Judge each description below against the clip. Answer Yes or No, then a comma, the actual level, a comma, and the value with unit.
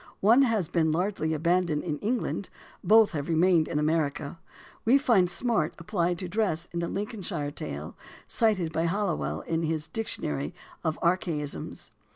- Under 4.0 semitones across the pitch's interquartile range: No, average, 4.5 semitones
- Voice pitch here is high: No, medium, 170 Hz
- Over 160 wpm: No, average, 150 wpm